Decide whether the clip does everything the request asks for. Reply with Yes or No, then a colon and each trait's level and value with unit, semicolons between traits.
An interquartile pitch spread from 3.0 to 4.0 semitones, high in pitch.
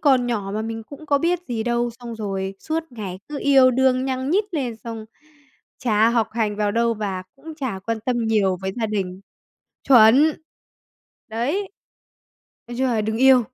Yes: average, 3.6 semitones; high, 235 Hz